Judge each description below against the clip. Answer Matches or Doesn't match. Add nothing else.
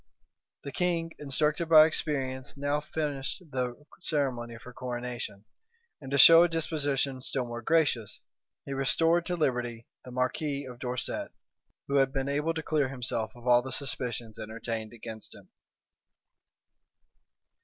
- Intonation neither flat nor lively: Matches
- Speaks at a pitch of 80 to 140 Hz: Matches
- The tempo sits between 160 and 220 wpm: Doesn't match